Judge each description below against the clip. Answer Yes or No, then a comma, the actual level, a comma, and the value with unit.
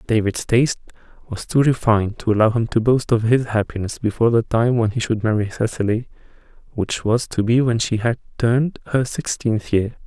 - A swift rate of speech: No, average, 190 wpm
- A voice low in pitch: Yes, low, 115 Hz